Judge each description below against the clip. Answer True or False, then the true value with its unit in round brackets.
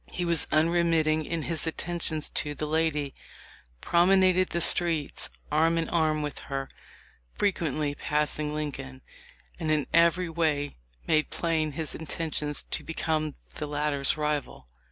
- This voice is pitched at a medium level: True (155 Hz)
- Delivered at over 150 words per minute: False (140 wpm)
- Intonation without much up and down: True (2.0 semitones)